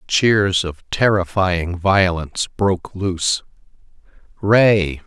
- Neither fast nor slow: No, slow, 85 wpm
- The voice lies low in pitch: Yes, very low, 95 Hz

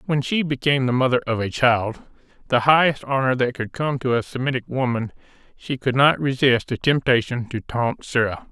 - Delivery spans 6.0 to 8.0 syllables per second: No, 5.3 syllables/s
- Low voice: Yes, low, 125 Hz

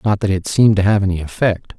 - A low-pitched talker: Yes, low, 100 Hz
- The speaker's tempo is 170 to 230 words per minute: No, fast, 270 wpm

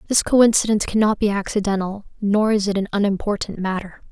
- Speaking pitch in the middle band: No, high, 205 Hz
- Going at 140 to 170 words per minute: Yes, average, 160 wpm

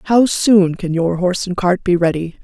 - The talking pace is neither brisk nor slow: No, fast, 220 wpm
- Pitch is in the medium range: Yes, medium, 180 Hz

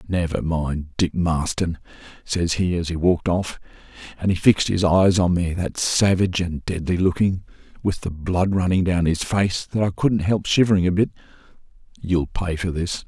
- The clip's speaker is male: Yes, male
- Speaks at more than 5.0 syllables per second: No, 4.9 syllables/s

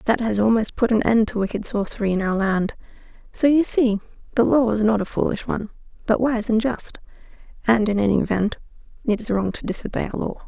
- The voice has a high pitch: Yes, high, 220 Hz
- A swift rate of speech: Yes, fast, 210 wpm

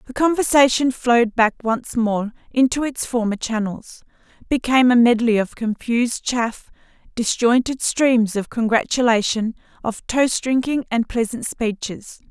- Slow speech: Yes, slow, 125 wpm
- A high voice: Yes, high, 235 Hz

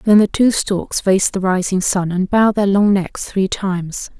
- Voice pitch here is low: No, high, 195 Hz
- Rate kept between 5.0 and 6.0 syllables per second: No, 4.6 syllables/s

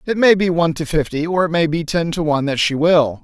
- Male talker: Yes, male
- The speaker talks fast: Yes, fast, 295 wpm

